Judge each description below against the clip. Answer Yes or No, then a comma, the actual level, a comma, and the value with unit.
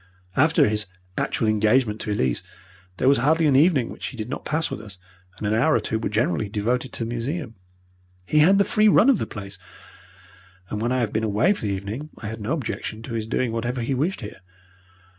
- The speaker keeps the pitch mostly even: No, average, 5.1 semitones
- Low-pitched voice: Yes, low, 115 Hz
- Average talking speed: No, fast, 225 wpm